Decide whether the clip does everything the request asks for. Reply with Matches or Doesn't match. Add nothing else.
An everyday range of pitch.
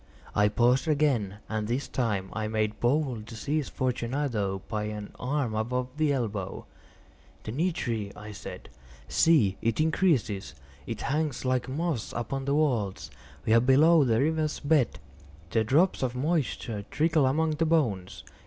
Doesn't match